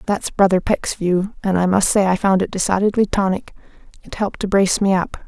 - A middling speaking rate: No, fast, 215 wpm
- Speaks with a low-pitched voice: No, high, 190 Hz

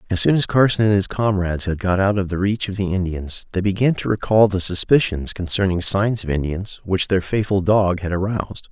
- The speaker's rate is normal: No, fast, 220 wpm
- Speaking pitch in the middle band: No, very low, 95 Hz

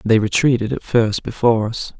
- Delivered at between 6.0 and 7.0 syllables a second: No, 5.4 syllables/s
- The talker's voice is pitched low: Yes, low, 115 Hz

